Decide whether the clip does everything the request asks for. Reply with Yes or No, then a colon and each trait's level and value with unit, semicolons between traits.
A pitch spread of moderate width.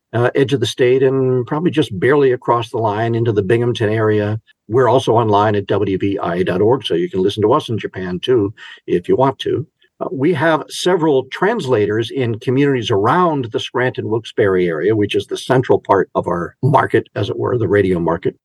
Yes: average, 3.9 semitones